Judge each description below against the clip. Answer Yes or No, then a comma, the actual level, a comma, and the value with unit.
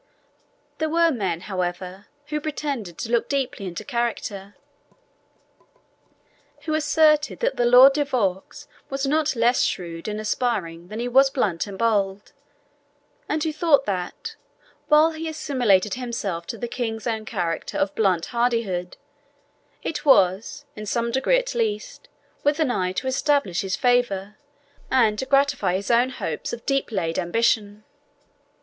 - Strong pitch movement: Yes, wide, 6.1 semitones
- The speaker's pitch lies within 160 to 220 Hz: No, high, 235 Hz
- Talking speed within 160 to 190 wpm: No, average, 145 wpm